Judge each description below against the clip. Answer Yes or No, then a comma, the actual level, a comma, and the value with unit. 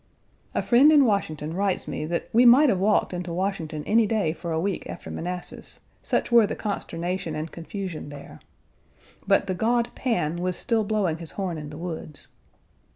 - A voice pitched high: No, medium, 180 Hz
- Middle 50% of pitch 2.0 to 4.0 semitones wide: No, average, 4.7 semitones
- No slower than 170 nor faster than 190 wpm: Yes, average, 180 wpm